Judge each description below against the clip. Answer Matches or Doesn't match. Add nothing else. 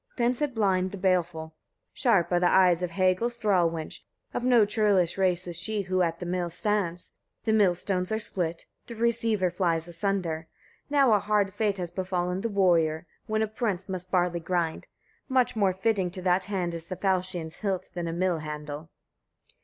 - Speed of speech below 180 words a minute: Doesn't match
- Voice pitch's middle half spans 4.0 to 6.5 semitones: Doesn't match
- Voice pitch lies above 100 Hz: Matches